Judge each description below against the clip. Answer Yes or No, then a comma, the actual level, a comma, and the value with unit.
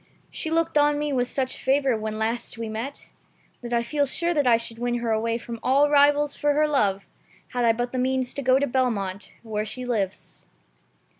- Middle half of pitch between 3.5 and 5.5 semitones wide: Yes, average, 3.8 semitones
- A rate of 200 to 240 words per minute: Yes, fast, 205 wpm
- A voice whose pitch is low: No, very high, 250 Hz